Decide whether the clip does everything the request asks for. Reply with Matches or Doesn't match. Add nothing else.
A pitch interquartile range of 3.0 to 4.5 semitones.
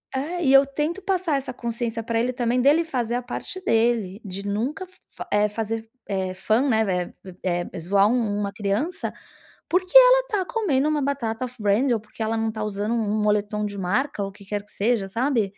Doesn't match